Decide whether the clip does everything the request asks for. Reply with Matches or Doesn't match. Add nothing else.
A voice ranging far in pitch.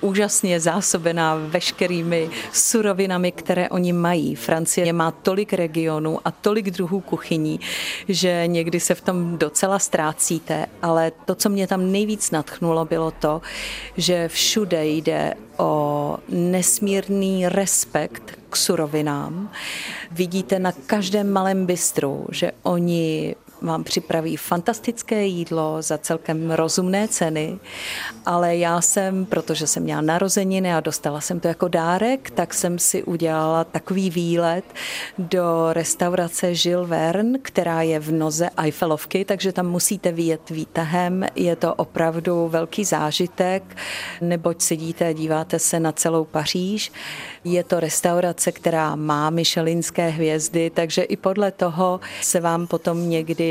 Doesn't match